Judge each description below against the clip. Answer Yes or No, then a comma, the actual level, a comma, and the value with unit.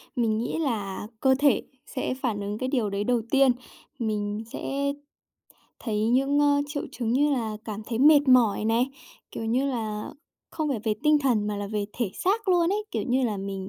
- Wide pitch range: No, average, 4.5 semitones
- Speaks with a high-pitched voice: Yes, high, 240 Hz